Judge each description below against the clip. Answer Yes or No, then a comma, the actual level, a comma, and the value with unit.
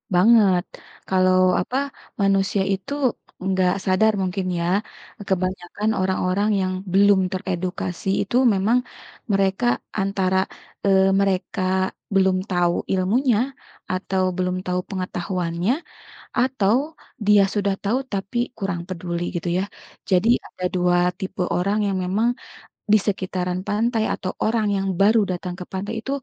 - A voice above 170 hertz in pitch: Yes, high, 190 Hz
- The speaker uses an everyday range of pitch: No, narrow, 1.8 semitones